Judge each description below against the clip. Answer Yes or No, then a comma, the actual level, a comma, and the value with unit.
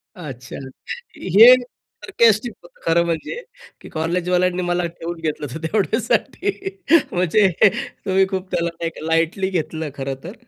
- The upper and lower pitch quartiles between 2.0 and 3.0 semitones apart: No, average, 4.3 semitones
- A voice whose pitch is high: No, medium, 180 Hz